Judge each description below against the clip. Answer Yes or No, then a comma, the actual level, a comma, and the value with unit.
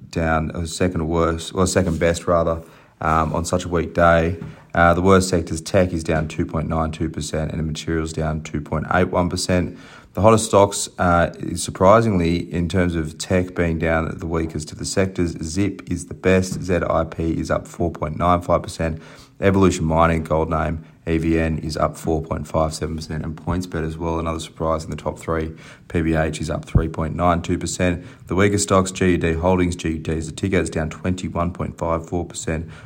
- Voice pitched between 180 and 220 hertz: No, very low, 85 Hz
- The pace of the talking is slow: No, average, 155 wpm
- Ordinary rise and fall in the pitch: No, narrow, 1.9 semitones